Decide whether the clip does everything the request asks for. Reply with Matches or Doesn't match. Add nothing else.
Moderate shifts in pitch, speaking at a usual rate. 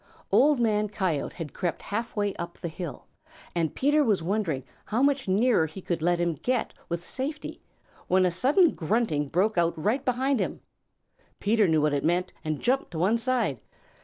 Doesn't match